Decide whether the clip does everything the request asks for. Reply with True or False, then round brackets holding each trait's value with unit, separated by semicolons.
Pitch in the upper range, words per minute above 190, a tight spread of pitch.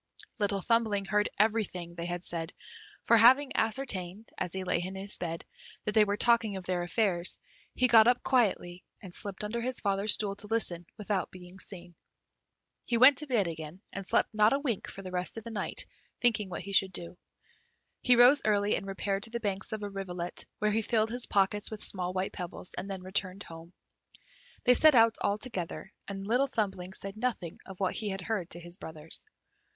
False (200 Hz; 200 wpm; 3.6 semitones)